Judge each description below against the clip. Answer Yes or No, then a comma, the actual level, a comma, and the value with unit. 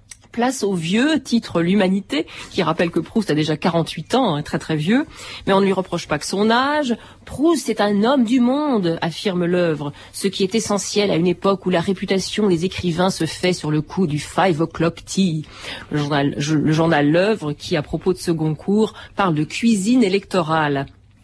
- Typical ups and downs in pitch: Yes, average, 4.6 semitones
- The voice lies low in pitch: No, medium, 185 Hz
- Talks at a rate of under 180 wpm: No, average, 200 wpm